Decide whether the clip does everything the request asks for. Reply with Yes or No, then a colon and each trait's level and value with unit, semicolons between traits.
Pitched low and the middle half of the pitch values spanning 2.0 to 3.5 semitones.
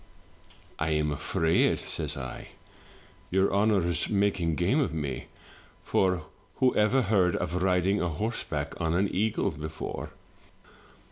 No: very low, 90 Hz; average, 4.2 semitones